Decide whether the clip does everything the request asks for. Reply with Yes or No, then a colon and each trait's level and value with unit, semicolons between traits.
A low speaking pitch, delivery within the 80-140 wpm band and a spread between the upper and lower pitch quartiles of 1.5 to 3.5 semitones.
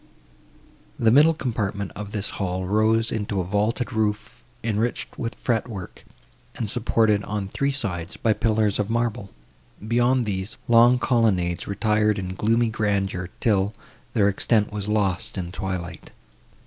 Yes: low, 105 Hz; slow, 135 wpm; average, 2.7 semitones